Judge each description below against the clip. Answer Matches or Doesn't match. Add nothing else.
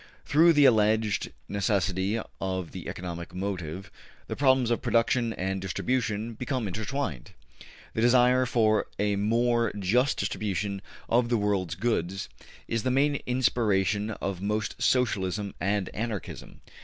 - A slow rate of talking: Matches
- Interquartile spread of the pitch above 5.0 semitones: Doesn't match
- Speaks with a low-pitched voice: Matches